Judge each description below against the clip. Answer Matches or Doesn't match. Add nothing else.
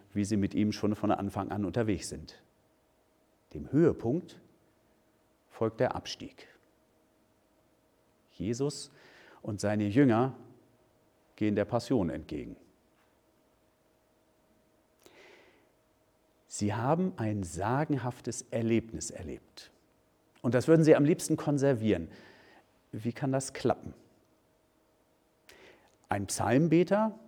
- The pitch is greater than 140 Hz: Doesn't match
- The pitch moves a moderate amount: Matches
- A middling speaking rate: Doesn't match